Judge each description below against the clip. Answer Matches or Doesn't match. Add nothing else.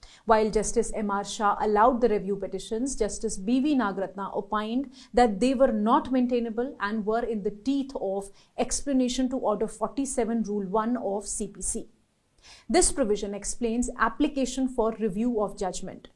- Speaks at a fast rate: Doesn't match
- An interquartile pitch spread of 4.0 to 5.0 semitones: Doesn't match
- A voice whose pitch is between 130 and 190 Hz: Doesn't match